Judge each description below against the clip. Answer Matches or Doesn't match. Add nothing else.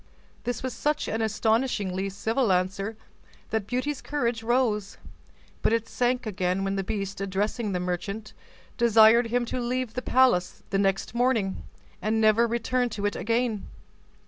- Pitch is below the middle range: Doesn't match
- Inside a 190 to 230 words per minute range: Doesn't match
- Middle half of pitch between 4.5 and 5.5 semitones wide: Doesn't match